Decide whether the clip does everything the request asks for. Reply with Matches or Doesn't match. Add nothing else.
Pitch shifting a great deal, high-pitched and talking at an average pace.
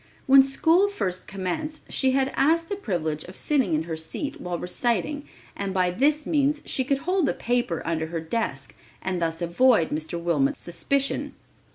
Matches